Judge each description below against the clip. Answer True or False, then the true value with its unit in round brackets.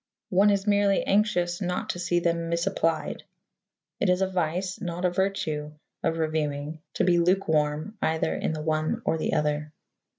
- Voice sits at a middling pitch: True (170 Hz)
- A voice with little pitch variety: False (3.2 semitones)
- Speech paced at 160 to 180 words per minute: True (165 wpm)